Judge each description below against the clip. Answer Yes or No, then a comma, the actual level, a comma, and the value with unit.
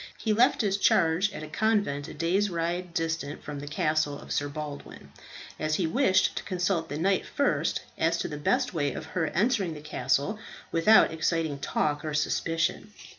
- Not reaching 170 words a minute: No, average, 180 wpm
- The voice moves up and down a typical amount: Yes, average, 4.2 semitones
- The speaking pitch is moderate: Yes, medium, 165 Hz